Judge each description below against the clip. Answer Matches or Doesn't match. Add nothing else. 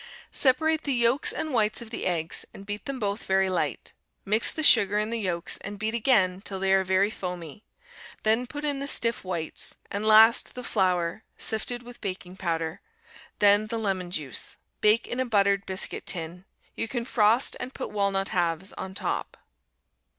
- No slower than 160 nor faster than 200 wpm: Matches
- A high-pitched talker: Matches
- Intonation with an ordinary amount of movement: Matches